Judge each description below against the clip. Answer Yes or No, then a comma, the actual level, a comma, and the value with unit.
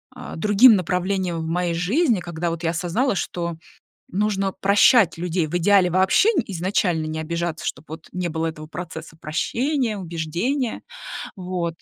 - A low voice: No, medium, 180 Hz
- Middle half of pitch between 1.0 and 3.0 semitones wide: No, average, 3.4 semitones